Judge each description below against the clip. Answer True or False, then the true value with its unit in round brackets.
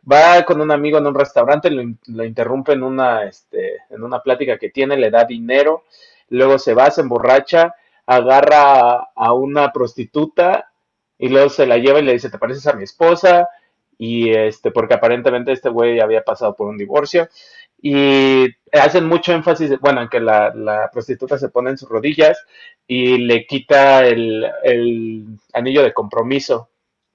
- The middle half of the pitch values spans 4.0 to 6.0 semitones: True (4.4 semitones)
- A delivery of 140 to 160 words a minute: False (175 wpm)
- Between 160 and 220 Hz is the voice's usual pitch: False (135 Hz)